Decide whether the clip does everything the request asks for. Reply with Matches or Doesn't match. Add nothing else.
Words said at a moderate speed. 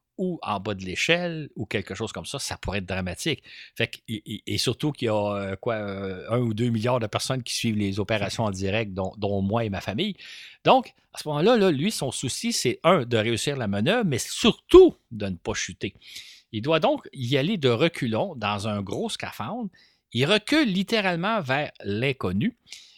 Matches